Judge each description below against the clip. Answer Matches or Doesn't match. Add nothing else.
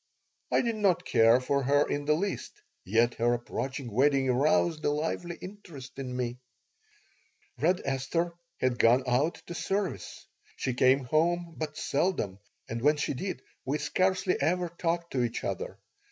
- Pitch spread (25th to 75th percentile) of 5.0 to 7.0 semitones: Matches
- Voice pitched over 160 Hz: Doesn't match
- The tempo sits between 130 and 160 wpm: Matches